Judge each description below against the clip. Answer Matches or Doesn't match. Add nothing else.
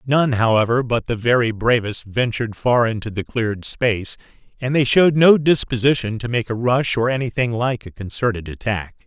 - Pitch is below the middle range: Matches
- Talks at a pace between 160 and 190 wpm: Matches